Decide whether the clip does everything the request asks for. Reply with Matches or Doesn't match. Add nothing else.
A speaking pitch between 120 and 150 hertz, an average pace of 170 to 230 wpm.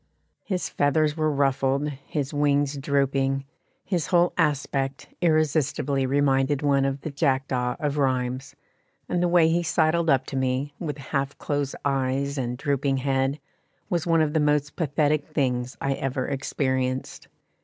Doesn't match